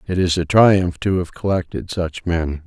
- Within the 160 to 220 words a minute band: Yes, average, 200 wpm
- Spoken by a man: Yes, male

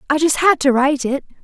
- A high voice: Yes, very high, 285 Hz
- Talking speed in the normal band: No, fast, 250 wpm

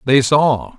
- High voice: No, low, 135 Hz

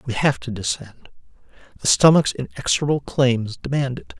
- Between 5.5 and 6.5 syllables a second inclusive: No, 5.1 syllables/s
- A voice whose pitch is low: Yes, low, 130 Hz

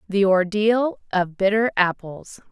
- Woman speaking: Yes, female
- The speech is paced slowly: Yes, slow, 120 wpm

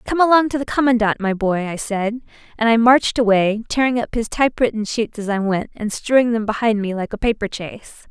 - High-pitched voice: Yes, high, 225 Hz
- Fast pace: Yes, fast, 220 wpm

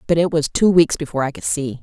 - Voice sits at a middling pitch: Yes, medium, 155 Hz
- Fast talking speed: Yes, fast, 295 wpm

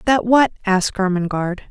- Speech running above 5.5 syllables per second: Yes, 5.8 syllables/s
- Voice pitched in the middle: No, high, 205 Hz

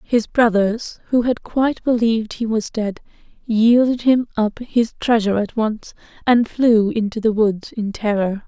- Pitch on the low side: No, high, 225 Hz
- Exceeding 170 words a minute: No, average, 165 wpm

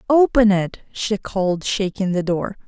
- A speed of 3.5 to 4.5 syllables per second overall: Yes, 4.3 syllables/s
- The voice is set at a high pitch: Yes, high, 200 Hz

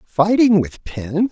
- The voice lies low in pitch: No, medium, 180 Hz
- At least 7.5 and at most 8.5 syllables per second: No, 3.4 syllables/s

